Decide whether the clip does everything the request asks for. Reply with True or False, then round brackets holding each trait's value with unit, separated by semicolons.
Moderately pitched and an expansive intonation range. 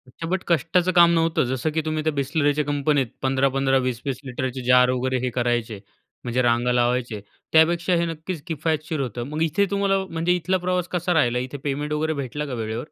False (145 Hz; 4.5 semitones)